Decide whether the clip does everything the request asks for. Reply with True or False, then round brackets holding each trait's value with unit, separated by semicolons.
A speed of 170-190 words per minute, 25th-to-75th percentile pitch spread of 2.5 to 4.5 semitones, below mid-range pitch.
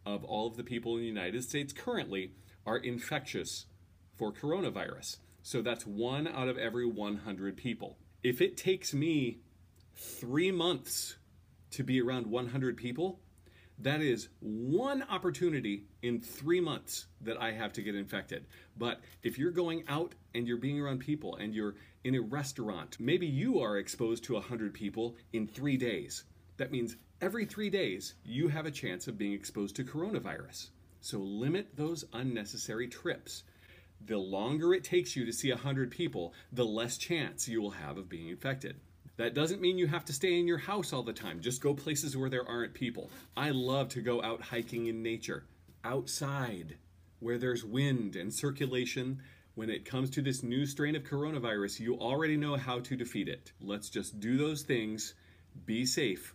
False (175 wpm; 5.6 semitones; 120 Hz)